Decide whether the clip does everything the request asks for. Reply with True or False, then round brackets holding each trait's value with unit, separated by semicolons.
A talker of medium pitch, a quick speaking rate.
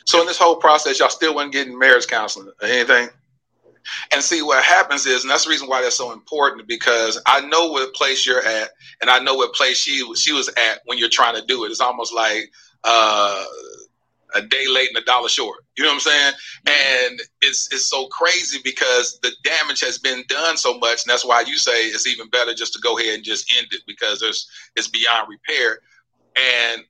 True (160 Hz; 220 wpm)